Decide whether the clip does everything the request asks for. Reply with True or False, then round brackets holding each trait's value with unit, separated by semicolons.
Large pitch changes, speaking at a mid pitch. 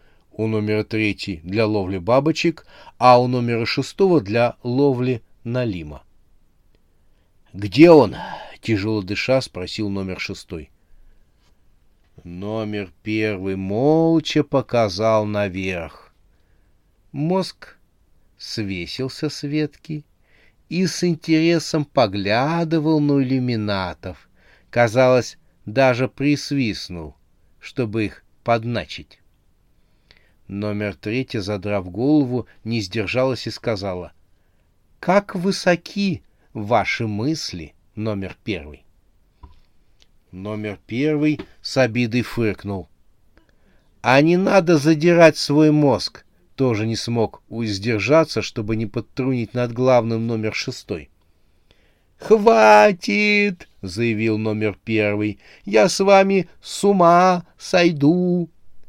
False (6.9 semitones; 110 Hz)